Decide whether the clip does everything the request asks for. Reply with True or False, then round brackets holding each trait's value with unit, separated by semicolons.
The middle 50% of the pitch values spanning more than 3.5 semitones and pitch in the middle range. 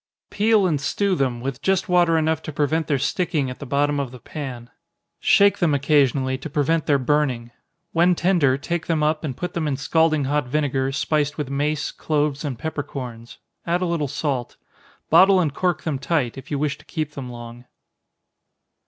False (3.2 semitones; 145 Hz)